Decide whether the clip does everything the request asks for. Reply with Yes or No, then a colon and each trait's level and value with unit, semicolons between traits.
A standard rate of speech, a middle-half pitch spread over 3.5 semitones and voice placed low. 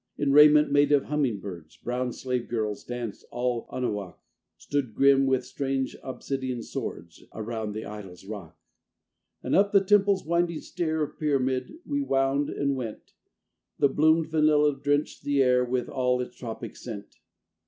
Yes: average, 155 wpm; average, 3.9 semitones; low, 130 Hz